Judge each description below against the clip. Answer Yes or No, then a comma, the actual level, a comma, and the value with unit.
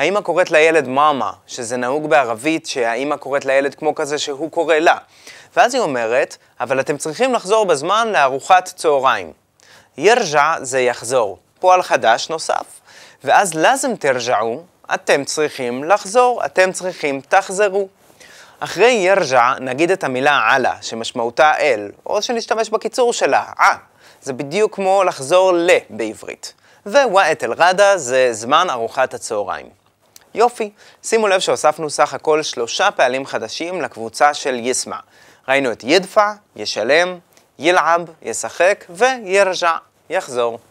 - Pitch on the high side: No, medium, 160 Hz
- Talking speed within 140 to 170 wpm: No, average, 125 wpm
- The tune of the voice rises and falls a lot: Yes, wide, 6.5 semitones